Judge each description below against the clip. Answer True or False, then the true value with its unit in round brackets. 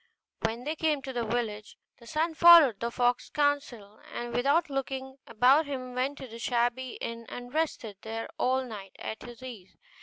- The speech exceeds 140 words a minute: True (180 wpm)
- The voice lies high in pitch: True (250 Hz)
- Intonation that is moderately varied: True (3.2 semitones)